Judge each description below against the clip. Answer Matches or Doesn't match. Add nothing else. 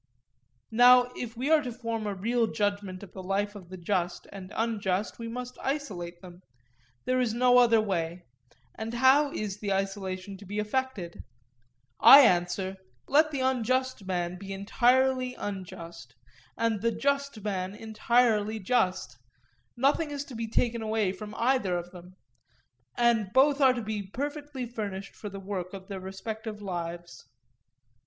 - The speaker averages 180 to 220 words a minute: Doesn't match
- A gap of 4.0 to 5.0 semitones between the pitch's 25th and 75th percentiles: Matches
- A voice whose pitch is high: Matches